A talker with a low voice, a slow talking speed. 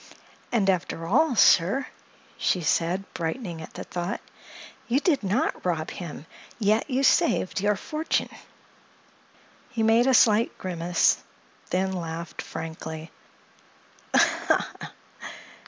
No: high, 190 Hz; slow, 110 wpm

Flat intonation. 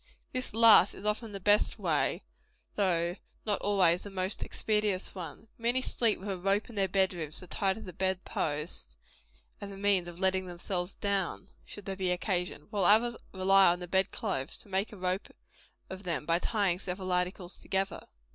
Yes: narrow, 2.3 semitones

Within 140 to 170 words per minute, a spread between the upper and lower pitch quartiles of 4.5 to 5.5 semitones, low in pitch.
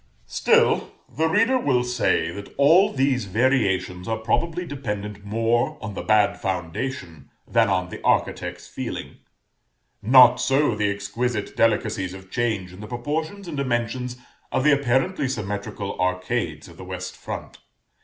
Yes: average, 145 wpm; average, 5.1 semitones; low, 115 Hz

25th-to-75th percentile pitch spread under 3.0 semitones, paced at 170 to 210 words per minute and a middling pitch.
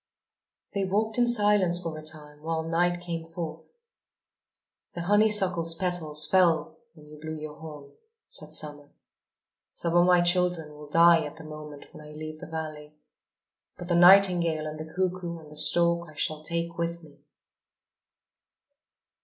No: narrow, 2.4 semitones; average, 155 wpm; medium, 165 Hz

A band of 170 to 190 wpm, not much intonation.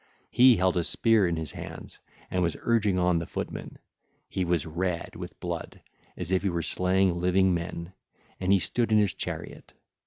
Yes: average, 185 wpm; narrow, 2.2 semitones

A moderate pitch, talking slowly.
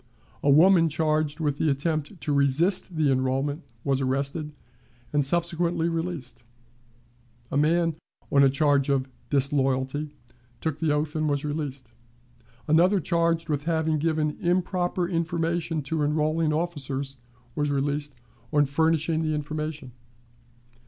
Yes: medium, 150 Hz; slow, 125 wpm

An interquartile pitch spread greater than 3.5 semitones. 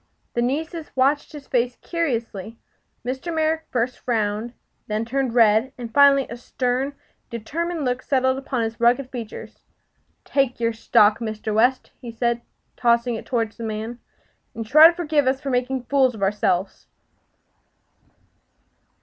No: average, 3.2 semitones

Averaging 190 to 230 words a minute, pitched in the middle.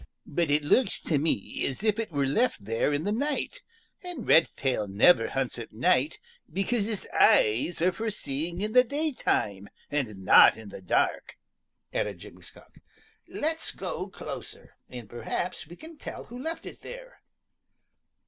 No: average, 160 wpm; medium, 165 Hz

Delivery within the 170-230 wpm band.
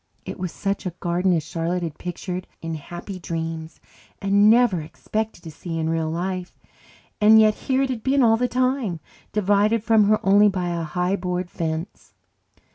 Yes: average, 180 wpm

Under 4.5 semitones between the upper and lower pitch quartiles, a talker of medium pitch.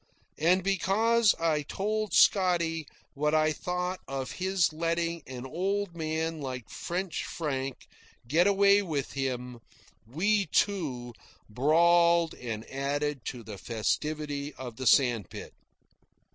No: average, 5.2 semitones; medium, 155 Hz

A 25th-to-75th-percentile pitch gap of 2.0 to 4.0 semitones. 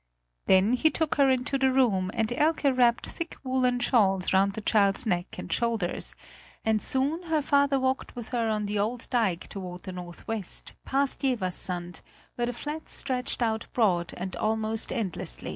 No: average, 5.1 semitones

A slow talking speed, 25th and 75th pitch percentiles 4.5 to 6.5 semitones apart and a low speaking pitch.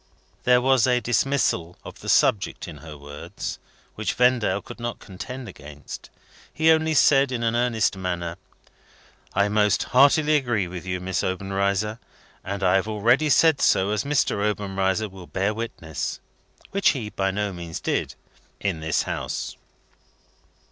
No: average, 150 wpm; average, 4.9 semitones; low, 105 Hz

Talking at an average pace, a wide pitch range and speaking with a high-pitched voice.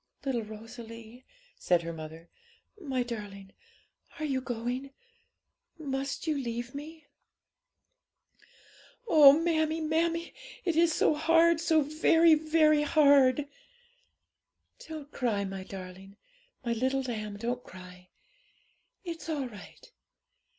No: slow, 110 wpm; wide, 6.0 semitones; very high, 270 Hz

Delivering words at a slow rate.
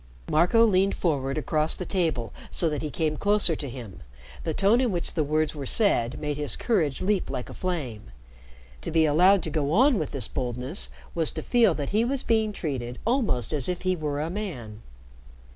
No: average, 200 wpm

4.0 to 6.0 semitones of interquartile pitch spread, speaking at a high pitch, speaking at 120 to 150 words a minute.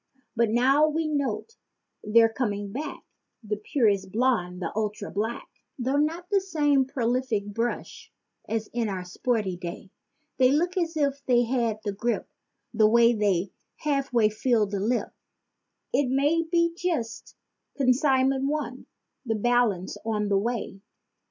Yes: average, 4.7 semitones; high, 240 Hz; average, 140 wpm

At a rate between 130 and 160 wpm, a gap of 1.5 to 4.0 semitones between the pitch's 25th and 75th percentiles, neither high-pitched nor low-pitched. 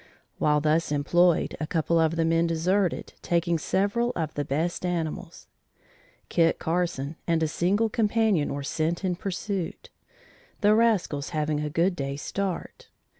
Yes: average, 145 wpm; average, 3.4 semitones; medium, 170 Hz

